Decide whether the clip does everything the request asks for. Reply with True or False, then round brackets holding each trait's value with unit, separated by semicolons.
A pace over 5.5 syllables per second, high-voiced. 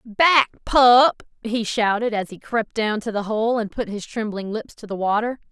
False (4.4 syllables/s; 220 Hz)